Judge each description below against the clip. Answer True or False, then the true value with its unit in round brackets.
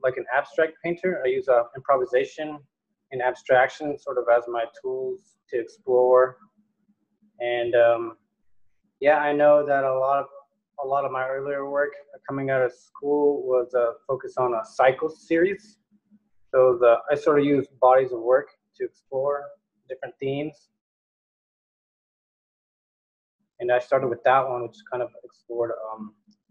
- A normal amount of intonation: False (6.5 semitones)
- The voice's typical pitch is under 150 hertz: True (140 Hz)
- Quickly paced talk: False (155 wpm)